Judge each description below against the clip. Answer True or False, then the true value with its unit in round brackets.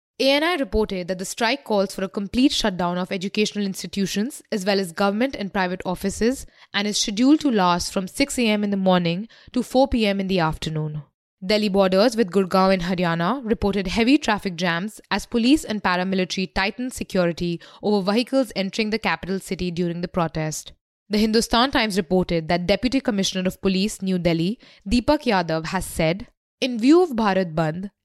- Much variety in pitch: False (3.7 semitones)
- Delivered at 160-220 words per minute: True (175 wpm)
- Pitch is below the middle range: False (200 Hz)